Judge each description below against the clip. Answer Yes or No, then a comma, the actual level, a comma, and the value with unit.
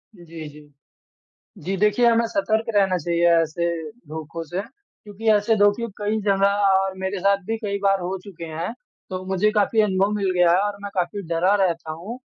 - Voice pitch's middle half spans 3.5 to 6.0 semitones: No, average, 3.1 semitones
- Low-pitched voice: No, high, 195 Hz